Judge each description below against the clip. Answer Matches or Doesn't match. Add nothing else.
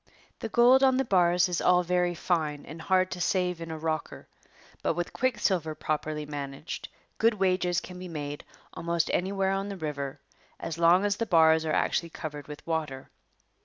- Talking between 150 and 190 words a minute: Matches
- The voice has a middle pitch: Matches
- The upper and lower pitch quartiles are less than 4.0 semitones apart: Matches